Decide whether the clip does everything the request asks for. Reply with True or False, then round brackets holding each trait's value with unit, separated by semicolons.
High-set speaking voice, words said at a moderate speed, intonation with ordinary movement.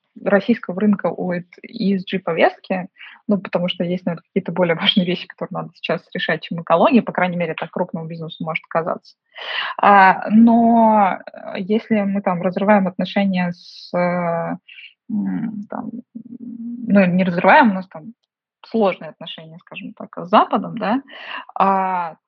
True (195 Hz; 135 wpm; 3.5 semitones)